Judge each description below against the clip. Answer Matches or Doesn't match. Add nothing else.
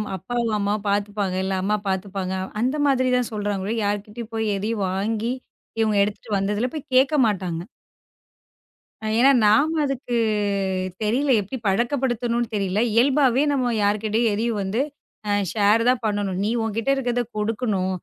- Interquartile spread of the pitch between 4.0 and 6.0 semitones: Doesn't match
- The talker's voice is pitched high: Matches